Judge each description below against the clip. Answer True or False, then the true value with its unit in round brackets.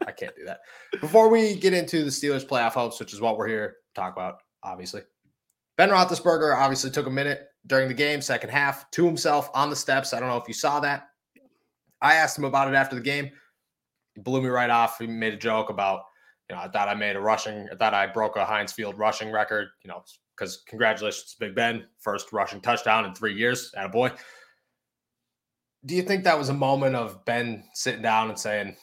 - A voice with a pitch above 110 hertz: True (135 Hz)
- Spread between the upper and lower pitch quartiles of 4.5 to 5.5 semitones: True (5.0 semitones)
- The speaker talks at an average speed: False (225 wpm)